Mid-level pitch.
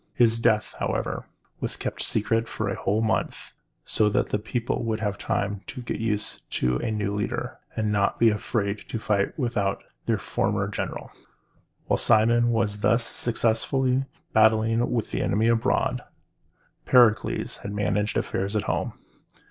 No: low, 110 Hz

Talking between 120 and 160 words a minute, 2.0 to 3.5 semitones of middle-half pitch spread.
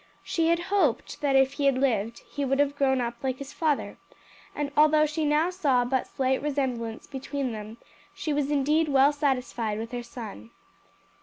No: average, 180 wpm; average, 3.1 semitones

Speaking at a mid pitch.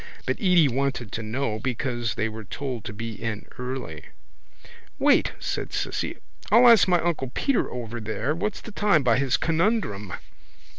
No: low, 130 Hz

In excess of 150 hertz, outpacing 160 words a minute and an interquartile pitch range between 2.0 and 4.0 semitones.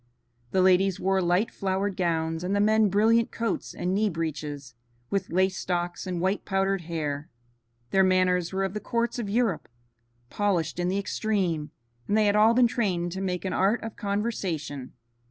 Yes: high, 190 Hz; average, 175 wpm; average, 2.9 semitones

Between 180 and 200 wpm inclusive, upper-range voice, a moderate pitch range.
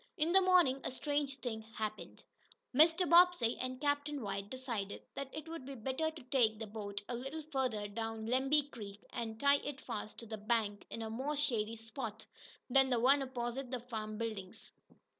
Yes: average, 185 wpm; very high, 250 Hz; average, 4.4 semitones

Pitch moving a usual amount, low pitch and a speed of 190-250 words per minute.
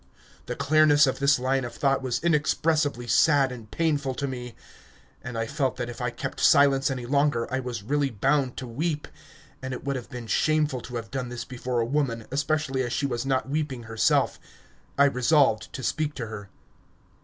Yes: average, 3.0 semitones; low, 130 Hz; average, 195 wpm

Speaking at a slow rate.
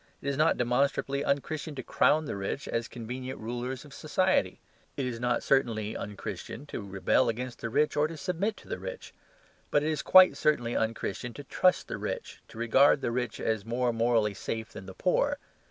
No: fast, 205 wpm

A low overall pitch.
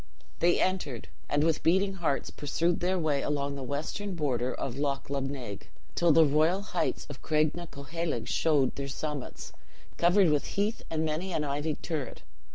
No: medium, 155 Hz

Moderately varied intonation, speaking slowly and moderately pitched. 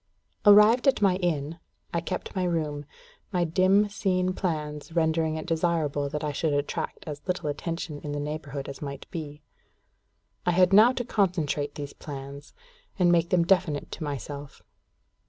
No: average, 3.8 semitones; average, 160 wpm; medium, 160 Hz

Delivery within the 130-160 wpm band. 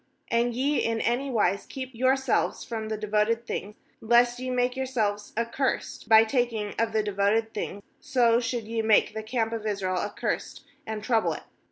No: average, 185 wpm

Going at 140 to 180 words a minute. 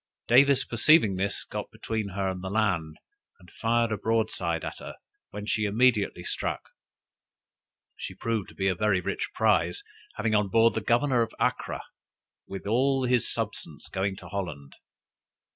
Yes: average, 160 wpm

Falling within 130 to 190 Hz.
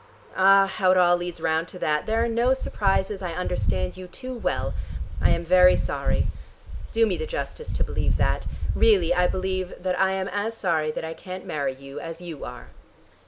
Yes: medium, 185 Hz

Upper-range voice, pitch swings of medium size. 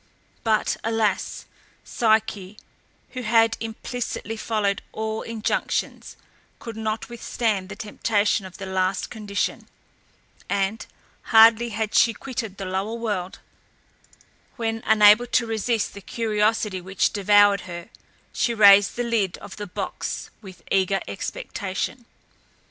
No: high, 215 Hz; narrow, 2.3 semitones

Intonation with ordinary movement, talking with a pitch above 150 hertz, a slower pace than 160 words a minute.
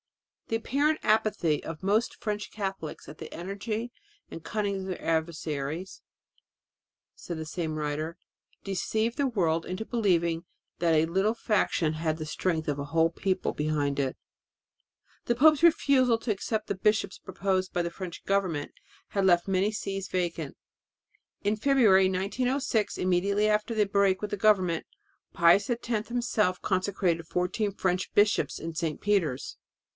Yes: average, 4.3 semitones; high, 190 Hz; average, 150 wpm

